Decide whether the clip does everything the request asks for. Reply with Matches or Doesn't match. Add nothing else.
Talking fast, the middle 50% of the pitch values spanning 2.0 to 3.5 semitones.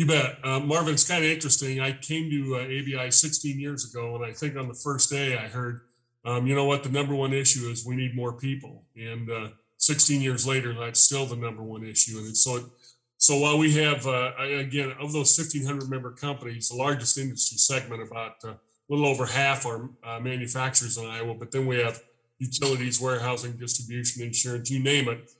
Matches